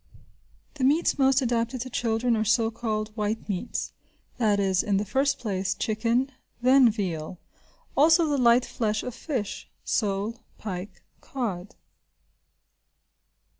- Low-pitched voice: No, high, 225 Hz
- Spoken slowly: Yes, slow, 130 wpm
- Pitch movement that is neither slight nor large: Yes, average, 3.7 semitones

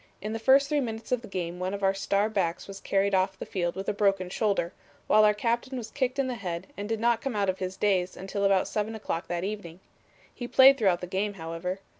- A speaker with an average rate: No, fast, 250 wpm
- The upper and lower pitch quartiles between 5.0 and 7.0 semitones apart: No, average, 3.2 semitones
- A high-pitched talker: Yes, high, 200 Hz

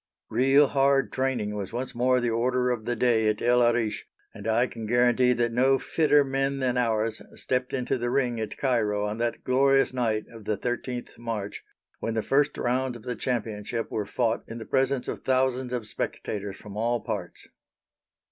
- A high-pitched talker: No, low, 120 Hz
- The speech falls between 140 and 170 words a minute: No, average, 185 wpm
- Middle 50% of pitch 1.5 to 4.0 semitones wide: Yes, narrow, 2.5 semitones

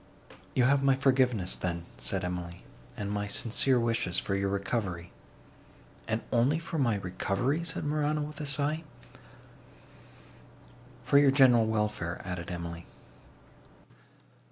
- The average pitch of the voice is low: Yes, low, 115 Hz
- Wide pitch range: Yes, wide, 7.0 semitones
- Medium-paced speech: No, slow, 125 wpm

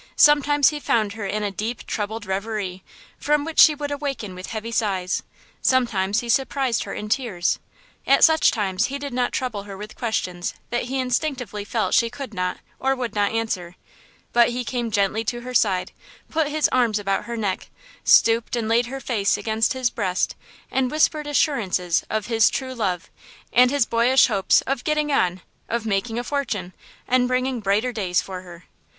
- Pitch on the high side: Yes, high, 230 Hz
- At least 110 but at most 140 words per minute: No, average, 185 wpm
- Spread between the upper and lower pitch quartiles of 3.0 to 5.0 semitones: Yes, average, 4.3 semitones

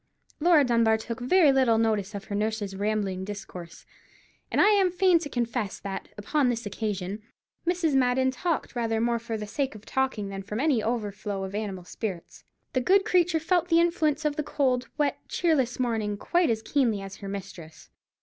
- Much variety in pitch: Yes, wide, 6.2 semitones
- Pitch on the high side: Yes, high, 235 Hz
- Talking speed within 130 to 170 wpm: No, average, 185 wpm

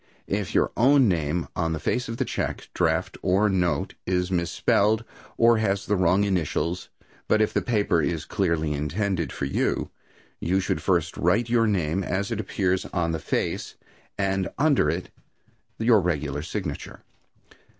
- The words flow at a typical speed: Yes, average, 160 wpm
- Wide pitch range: No, average, 4.0 semitones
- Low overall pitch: Yes, very low, 95 Hz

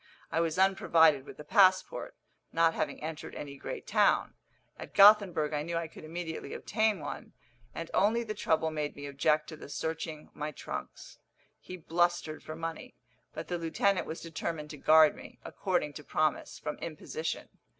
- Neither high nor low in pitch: Yes, medium, 160 Hz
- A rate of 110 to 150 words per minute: No, average, 170 wpm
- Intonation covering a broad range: No, narrow, 2.4 semitones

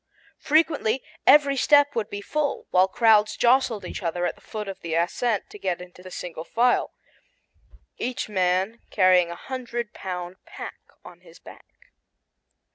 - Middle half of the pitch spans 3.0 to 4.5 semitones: No, wide, 5.4 semitones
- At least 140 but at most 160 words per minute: Yes, average, 155 wpm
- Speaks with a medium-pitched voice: No, high, 210 Hz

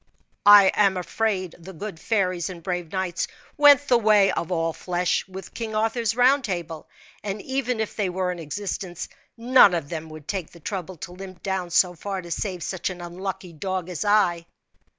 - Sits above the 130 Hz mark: Yes, medium, 185 Hz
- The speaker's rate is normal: Yes, average, 190 wpm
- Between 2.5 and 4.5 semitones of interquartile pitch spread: Yes, average, 3.2 semitones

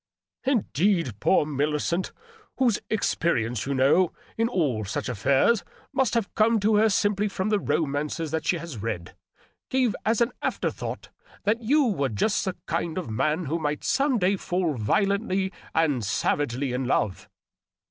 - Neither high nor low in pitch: Yes, medium, 170 Hz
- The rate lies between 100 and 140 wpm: No, average, 175 wpm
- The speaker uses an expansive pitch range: Yes, wide, 7.4 semitones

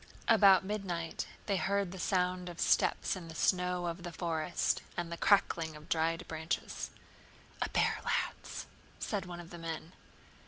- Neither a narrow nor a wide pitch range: No, narrow, 2.1 semitones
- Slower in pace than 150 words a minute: No, average, 160 wpm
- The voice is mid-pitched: Yes, medium, 175 Hz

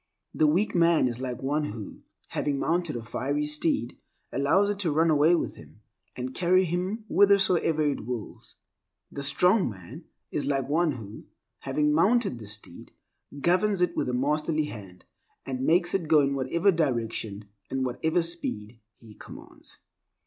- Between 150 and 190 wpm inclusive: Yes, average, 165 wpm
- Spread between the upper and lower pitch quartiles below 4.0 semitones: No, wide, 5.5 semitones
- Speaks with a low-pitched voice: No, medium, 150 Hz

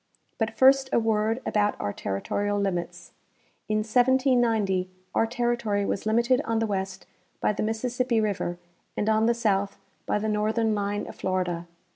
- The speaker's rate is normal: Yes, average, 160 wpm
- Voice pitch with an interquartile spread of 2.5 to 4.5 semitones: Yes, average, 2.8 semitones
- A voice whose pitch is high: Yes, high, 215 Hz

